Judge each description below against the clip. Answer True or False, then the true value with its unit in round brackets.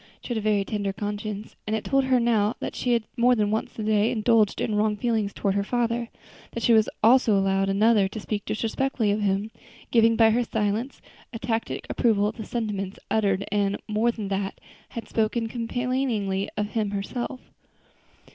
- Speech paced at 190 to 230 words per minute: True (195 wpm)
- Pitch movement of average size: False (2.3 semitones)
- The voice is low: False (215 Hz)